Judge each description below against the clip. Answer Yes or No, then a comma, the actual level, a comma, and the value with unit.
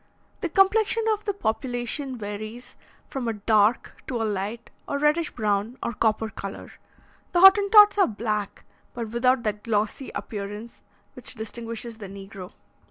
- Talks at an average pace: Yes, average, 145 wpm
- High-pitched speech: Yes, high, 230 Hz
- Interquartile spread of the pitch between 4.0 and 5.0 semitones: Yes, average, 4.4 semitones